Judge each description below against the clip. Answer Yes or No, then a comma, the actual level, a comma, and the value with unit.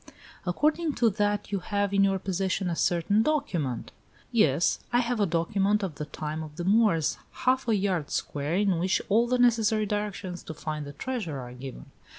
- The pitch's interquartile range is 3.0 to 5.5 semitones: Yes, average, 5.0 semitones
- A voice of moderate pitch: No, high, 195 Hz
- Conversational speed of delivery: Yes, average, 190 wpm